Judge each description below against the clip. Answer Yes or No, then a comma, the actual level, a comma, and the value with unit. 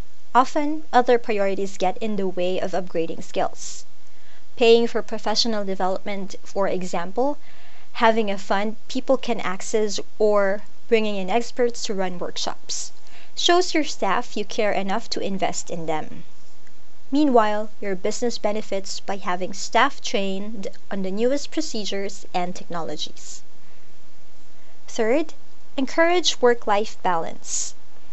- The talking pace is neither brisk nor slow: No, slow, 125 wpm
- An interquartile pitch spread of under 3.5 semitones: No, average, 3.8 semitones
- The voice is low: No, high, 215 Hz